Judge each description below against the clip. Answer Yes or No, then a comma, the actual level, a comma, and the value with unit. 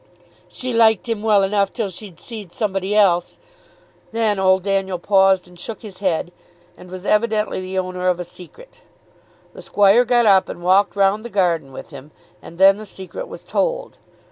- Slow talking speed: No, average, 180 wpm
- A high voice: Yes, high, 195 Hz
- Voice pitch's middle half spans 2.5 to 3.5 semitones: Yes, average, 2.8 semitones